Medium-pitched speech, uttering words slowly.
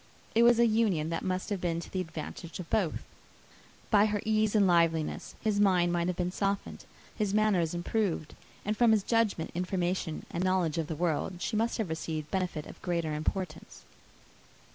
No: medium, 180 Hz; average, 185 wpm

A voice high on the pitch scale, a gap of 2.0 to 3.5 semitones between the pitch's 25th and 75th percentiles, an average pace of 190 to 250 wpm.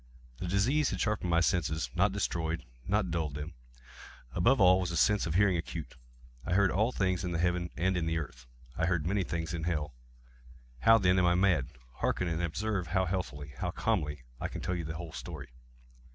No: very low, 90 Hz; average, 2.7 semitones; average, 195 wpm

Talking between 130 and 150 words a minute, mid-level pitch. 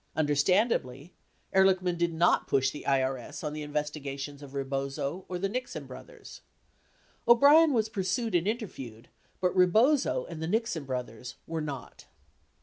Yes: average, 140 wpm; medium, 160 Hz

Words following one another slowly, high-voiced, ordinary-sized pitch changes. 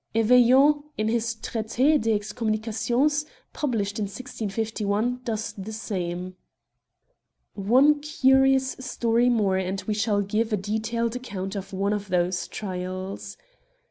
Yes: slow, 130 wpm; high, 220 Hz; average, 3.7 semitones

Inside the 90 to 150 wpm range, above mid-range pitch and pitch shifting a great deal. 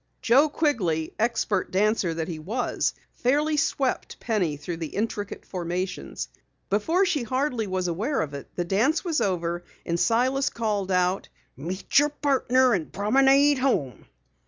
Yes: average, 145 wpm; high, 215 Hz; wide, 7.2 semitones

